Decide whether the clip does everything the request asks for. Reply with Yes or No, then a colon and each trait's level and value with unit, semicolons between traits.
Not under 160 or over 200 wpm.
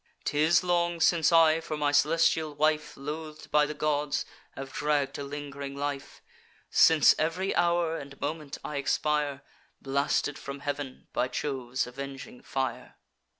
No: average, 140 wpm